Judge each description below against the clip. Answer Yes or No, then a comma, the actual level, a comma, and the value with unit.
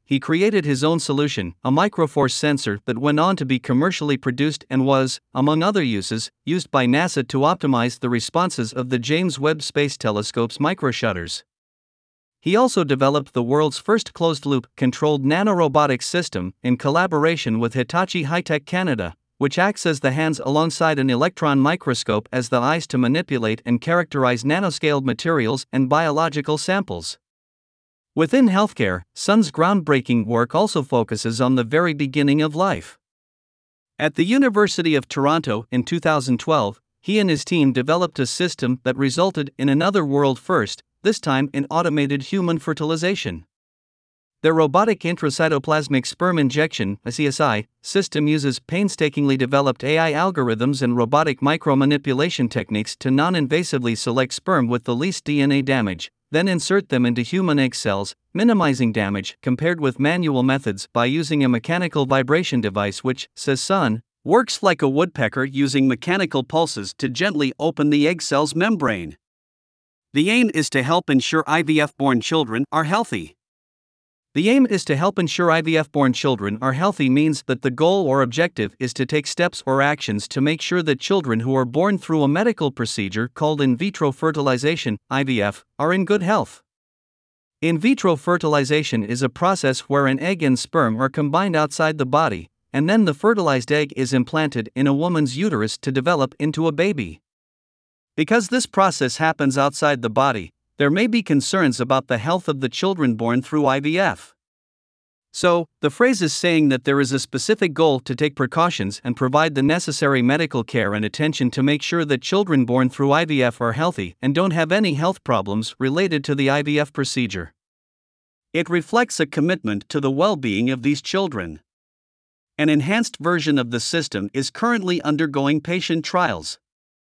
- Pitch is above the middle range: No, medium, 145 Hz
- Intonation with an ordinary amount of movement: Yes, average, 4.5 semitones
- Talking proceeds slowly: Yes, slow, 160 wpm